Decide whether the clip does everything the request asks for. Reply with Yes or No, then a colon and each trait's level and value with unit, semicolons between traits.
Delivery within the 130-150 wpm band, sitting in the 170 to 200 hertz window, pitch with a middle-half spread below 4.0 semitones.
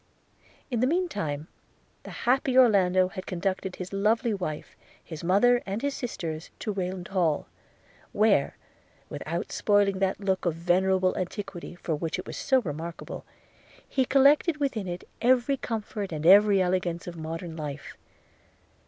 No: average, 145 wpm; high, 190 Hz; average, 4.7 semitones